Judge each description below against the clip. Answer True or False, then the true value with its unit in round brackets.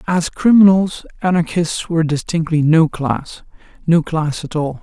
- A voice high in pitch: False (165 Hz)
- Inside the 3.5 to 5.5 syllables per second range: True (4.4 syllables/s)